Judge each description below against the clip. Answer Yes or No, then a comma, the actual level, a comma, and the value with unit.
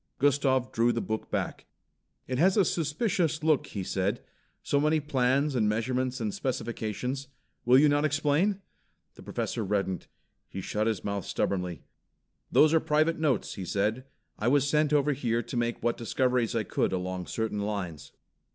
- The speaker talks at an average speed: Yes, average, 165 wpm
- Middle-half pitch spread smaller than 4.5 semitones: No, wide, 5.5 semitones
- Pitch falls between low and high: No, low, 125 Hz